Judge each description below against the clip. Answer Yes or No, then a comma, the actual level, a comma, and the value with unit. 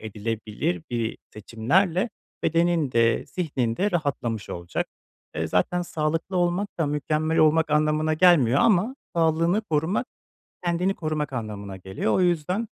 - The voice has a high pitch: No, medium, 155 Hz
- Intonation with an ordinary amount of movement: No, wide, 7.2 semitones